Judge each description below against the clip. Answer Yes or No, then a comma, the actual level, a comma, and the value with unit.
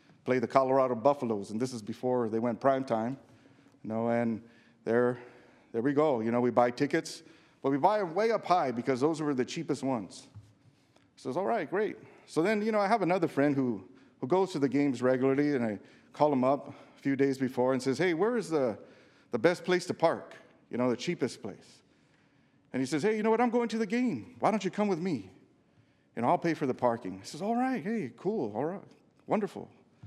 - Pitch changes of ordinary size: No, wide, 5.8 semitones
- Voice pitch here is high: No, low, 135 Hz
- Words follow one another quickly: Yes, fast, 230 wpm